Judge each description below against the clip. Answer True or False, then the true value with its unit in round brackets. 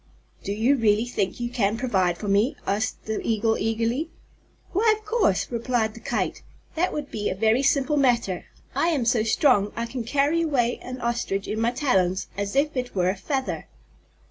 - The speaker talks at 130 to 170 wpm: False (190 wpm)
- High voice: True (235 Hz)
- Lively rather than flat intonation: False (4.7 semitones)